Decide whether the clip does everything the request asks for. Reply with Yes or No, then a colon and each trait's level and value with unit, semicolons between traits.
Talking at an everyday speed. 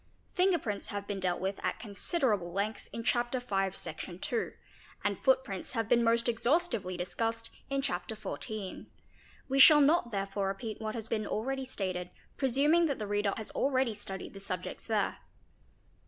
Yes: average, 165 wpm